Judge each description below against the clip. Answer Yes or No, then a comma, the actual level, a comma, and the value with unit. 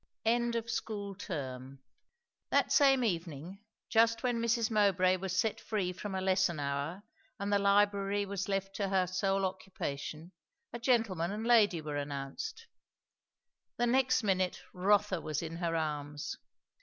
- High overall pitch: Yes, high, 195 Hz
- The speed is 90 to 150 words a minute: Yes, average, 145 wpm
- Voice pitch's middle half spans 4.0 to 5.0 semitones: Yes, average, 4.6 semitones